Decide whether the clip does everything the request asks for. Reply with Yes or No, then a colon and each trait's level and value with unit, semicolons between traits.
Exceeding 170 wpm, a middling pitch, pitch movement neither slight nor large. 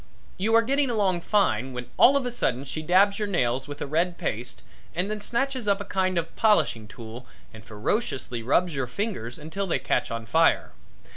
No: fast, 205 wpm; medium, 175 Hz; wide, 8.8 semitones